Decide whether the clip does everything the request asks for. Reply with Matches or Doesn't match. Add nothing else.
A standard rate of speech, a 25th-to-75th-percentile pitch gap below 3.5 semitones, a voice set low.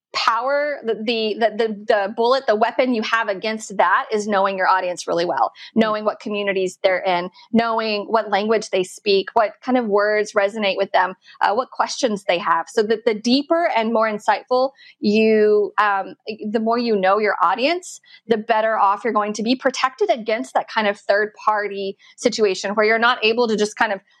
Doesn't match